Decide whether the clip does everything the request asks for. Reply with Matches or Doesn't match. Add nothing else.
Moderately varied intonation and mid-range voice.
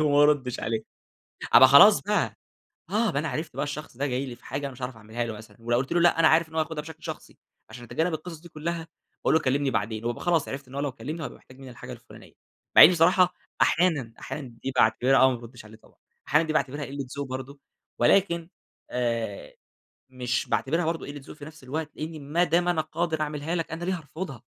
Matches